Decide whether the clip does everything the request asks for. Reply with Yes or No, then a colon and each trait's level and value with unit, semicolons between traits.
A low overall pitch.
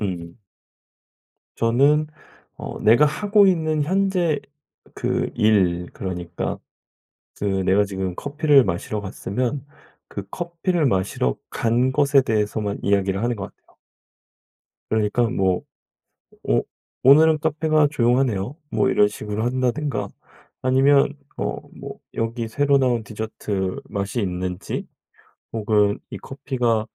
Yes: low, 115 Hz